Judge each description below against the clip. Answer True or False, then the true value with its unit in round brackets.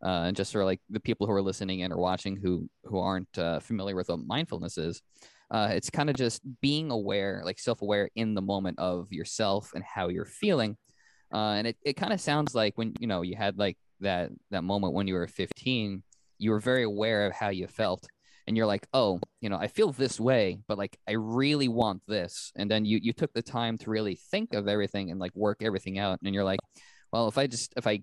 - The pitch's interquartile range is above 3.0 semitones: True (3.4 semitones)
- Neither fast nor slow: False (240 wpm)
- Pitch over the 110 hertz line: False (105 Hz)